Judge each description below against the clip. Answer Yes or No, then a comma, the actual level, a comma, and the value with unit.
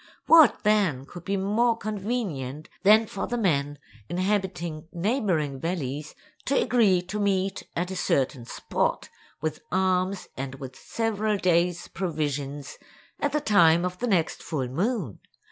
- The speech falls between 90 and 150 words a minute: Yes, average, 140 wpm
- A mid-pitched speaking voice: Yes, medium, 180 Hz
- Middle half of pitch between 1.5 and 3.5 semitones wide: No, wide, 5.4 semitones